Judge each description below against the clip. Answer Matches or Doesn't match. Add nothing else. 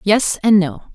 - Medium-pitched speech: Doesn't match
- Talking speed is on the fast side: Doesn't match